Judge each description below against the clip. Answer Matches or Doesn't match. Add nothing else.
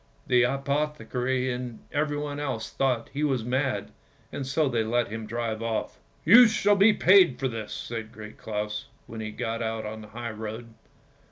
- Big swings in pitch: Doesn't match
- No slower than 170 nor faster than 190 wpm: Matches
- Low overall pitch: Matches